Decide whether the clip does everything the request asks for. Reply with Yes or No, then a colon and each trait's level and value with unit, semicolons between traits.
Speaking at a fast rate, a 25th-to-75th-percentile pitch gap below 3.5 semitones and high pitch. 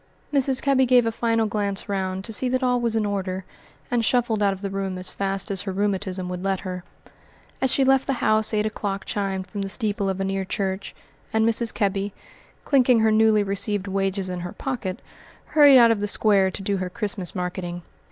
Yes: fast, 210 wpm; average, 2.9 semitones; high, 200 Hz